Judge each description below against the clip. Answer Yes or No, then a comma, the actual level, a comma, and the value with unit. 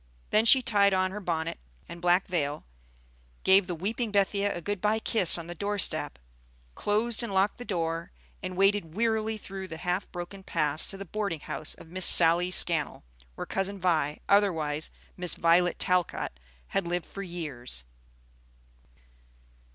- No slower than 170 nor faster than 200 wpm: No, average, 160 wpm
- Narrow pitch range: No, average, 3.4 semitones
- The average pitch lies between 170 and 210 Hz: Yes, medium, 185 Hz